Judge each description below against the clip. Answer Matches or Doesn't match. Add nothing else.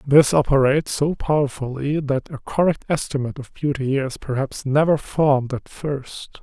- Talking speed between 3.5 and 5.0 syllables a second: Matches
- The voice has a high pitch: Doesn't match